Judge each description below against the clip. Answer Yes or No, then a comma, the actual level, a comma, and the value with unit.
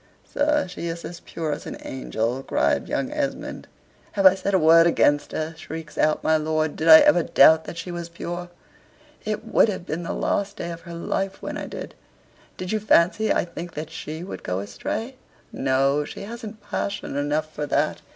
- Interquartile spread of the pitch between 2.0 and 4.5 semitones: Yes, average, 3.9 semitones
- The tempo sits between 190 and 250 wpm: Yes, average, 200 wpm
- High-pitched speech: No, medium, 170 Hz